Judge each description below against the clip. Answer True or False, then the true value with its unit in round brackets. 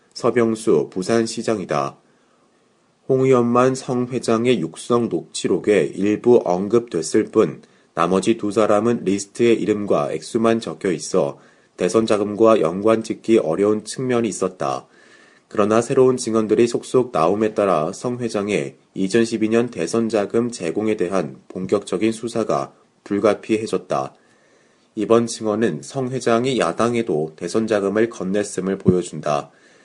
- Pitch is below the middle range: True (110 Hz)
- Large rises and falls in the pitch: False (2.7 semitones)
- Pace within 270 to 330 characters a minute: True (280 characters per minute)